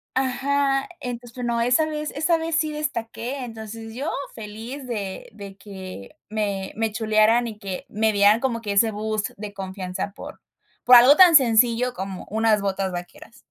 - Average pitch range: Yes, average, 3.7 semitones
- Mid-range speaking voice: No, high, 225 Hz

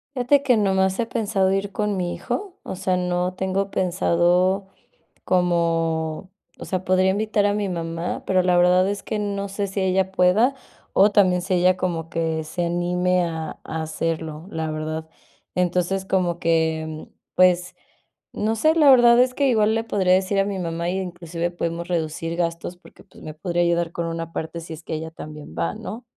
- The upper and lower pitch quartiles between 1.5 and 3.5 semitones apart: Yes, average, 2.8 semitones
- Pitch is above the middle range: No, medium, 180 Hz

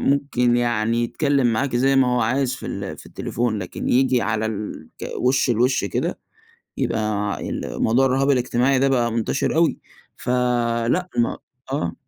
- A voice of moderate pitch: No, low, 125 Hz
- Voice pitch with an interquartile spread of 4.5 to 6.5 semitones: No, average, 2.7 semitones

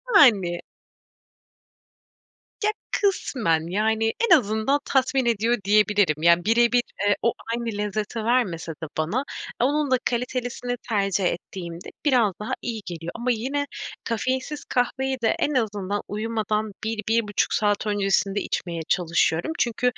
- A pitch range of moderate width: Yes, average, 3.8 semitones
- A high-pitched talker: Yes, high, 220 Hz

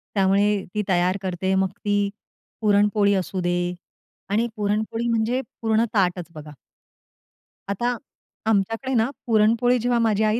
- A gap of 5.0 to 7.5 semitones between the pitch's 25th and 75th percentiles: No, average, 2.9 semitones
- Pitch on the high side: Yes, high, 210 Hz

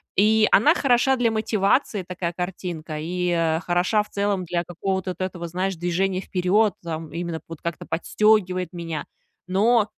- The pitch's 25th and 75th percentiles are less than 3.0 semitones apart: No, average, 3.3 semitones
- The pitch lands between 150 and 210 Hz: Yes, medium, 185 Hz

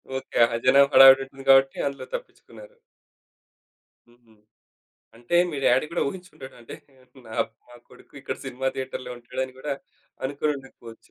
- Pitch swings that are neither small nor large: No, narrow, 2.0 semitones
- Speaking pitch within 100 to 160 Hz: Yes, low, 135 Hz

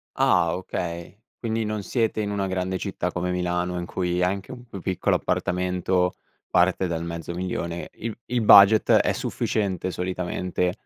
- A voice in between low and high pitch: No, very low, 90 Hz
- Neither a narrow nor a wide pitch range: No, narrow, 2.1 semitones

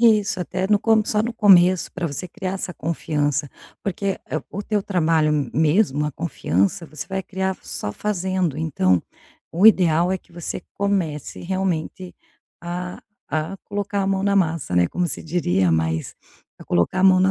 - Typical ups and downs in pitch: Yes, average, 4.0 semitones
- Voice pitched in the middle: Yes, medium, 180 Hz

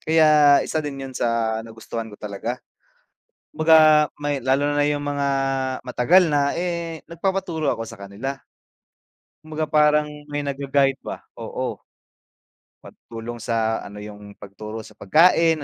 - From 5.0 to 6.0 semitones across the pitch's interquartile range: Yes, average, 5.3 semitones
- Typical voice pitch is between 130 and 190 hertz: Yes, medium, 140 Hz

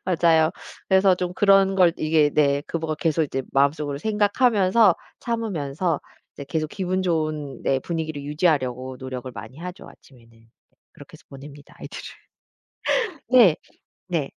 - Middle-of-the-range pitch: Yes, medium, 160 Hz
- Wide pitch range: No, average, 4.7 semitones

